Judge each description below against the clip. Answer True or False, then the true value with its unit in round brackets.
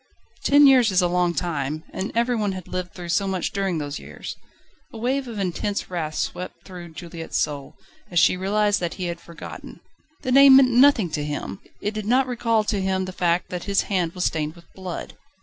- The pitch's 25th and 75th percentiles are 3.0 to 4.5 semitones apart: True (4.1 semitones)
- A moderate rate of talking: False (210 wpm)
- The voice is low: False (185 Hz)